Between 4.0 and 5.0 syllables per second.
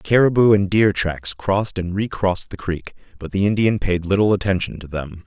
No: 5.2 syllables/s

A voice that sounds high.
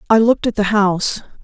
Yes: high, 210 Hz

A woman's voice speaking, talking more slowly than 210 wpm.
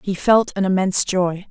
Yes: female; average, 200 wpm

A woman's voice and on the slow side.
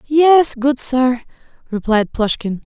Yes: female; slow, 110 wpm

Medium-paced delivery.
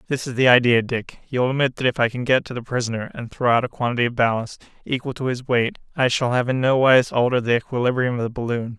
No: fast, 260 wpm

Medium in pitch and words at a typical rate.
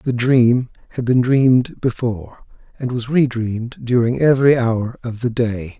No: low, 120 Hz; average, 165 wpm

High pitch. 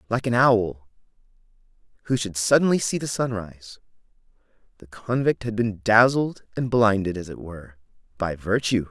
No: low, 110 Hz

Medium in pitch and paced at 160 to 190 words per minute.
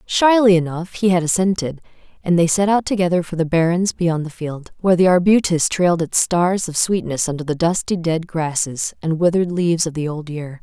No: medium, 170 Hz; fast, 205 wpm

